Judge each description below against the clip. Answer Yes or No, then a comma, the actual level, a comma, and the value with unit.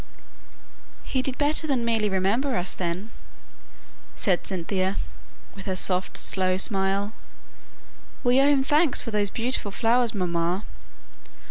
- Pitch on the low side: No, high, 205 Hz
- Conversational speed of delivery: No, slow, 125 wpm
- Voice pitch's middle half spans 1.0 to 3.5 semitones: No, average, 5.0 semitones